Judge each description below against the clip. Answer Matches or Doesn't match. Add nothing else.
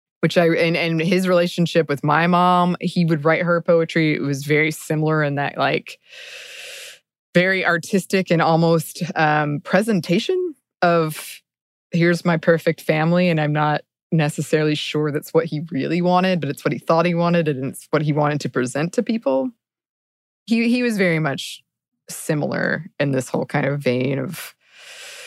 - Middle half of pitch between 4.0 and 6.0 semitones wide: Doesn't match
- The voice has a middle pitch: Matches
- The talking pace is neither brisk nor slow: Matches